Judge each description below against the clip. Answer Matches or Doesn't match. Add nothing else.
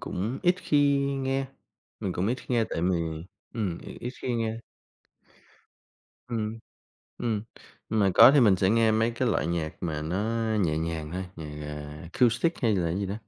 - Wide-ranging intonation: Matches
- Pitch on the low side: Matches